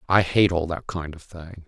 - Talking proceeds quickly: Yes, fast, 250 wpm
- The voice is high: No, very low, 85 Hz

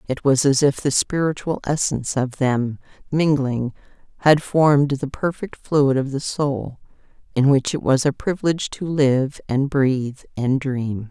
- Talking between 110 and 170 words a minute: Yes, average, 160 wpm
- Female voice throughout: Yes, female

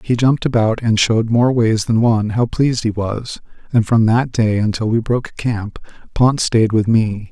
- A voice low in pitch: Yes, low, 115 Hz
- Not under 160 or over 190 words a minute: No, fast, 205 wpm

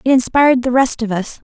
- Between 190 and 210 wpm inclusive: No, fast, 240 wpm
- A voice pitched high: Yes, very high, 250 Hz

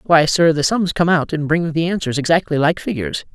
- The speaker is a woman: No, male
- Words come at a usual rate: No, fast, 235 wpm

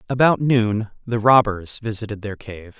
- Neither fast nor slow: Yes, average, 150 wpm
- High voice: No, low, 110 Hz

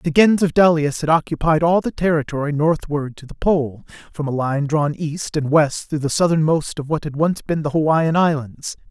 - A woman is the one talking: No, male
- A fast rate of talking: Yes, fast, 210 wpm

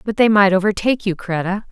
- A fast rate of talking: Yes, fast, 210 wpm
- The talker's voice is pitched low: No, high, 200 Hz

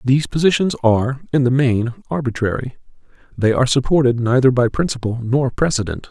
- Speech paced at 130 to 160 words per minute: Yes, average, 145 wpm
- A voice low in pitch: Yes, low, 130 Hz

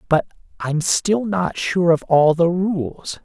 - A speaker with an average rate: Yes, average, 165 wpm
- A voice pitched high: No, medium, 170 Hz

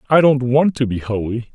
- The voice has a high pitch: No, low, 125 Hz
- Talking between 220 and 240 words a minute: Yes, fast, 235 wpm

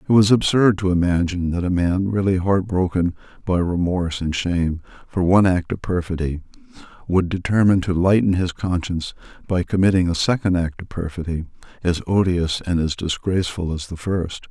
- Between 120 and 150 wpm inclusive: No, average, 165 wpm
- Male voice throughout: Yes, male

